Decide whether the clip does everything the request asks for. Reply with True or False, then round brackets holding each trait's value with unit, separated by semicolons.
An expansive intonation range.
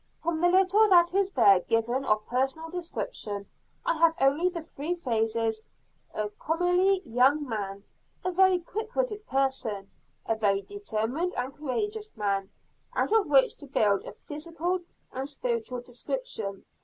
True (8.3 semitones)